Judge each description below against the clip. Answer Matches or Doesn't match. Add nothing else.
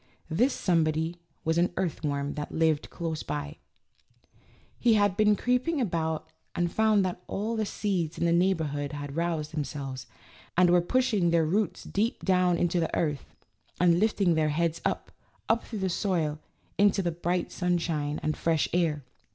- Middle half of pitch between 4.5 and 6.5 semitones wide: Doesn't match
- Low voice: Doesn't match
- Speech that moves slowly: Doesn't match